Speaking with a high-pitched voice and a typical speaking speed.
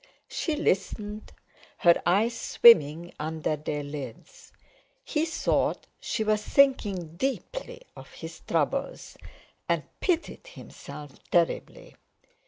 No: high, 205 Hz; slow, 100 wpm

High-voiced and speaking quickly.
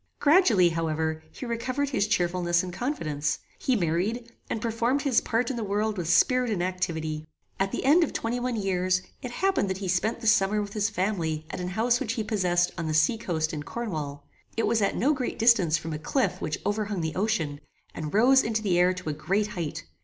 Yes: high, 200 Hz; fast, 215 wpm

